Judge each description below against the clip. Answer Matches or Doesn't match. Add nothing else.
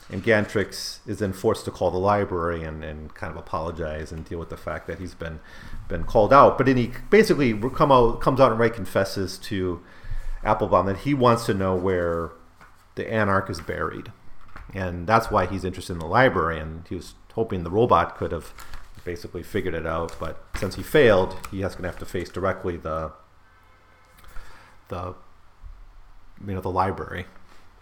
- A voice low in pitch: Matches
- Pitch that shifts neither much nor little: Matches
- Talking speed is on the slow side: Doesn't match